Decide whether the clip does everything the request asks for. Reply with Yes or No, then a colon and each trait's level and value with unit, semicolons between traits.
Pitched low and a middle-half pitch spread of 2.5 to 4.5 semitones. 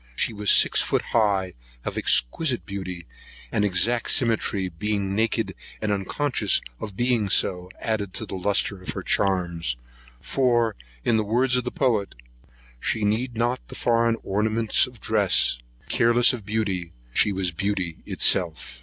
Yes: low, 105 Hz; average, 3.6 semitones